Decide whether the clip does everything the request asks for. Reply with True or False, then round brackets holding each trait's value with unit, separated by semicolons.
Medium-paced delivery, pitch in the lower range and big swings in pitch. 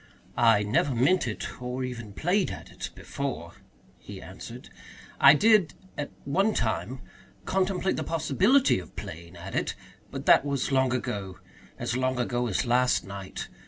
True (155 wpm; 130 Hz; 5.8 semitones)